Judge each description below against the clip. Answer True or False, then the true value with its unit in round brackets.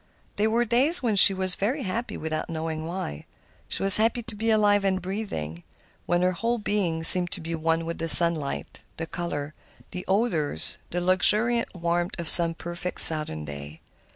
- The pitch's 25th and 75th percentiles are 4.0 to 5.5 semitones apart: True (4.4 semitones)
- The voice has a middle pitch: True (180 Hz)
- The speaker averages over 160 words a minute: True (180 wpm)